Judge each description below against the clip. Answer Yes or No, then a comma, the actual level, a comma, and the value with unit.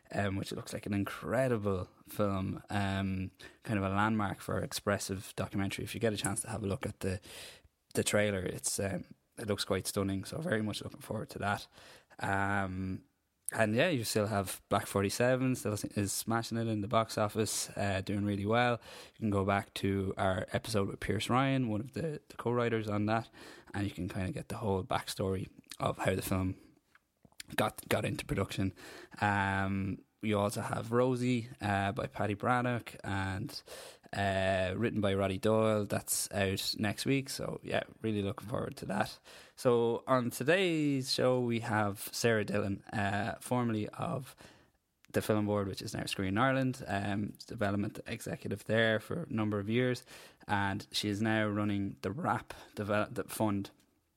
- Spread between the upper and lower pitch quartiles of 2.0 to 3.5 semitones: Yes, average, 2.8 semitones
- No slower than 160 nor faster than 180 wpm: Yes, average, 175 wpm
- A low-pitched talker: Yes, low, 105 Hz